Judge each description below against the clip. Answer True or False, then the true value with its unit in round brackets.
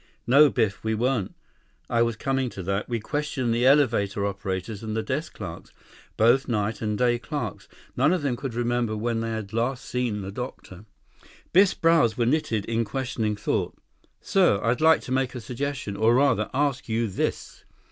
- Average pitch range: True (3.7 semitones)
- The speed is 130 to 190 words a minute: True (180 wpm)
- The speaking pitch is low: True (120 Hz)